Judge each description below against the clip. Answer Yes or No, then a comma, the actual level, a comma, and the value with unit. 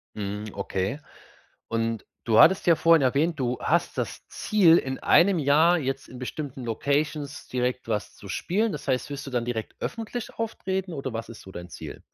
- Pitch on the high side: No, low, 135 Hz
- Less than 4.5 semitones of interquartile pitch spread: No, wide, 6.3 semitones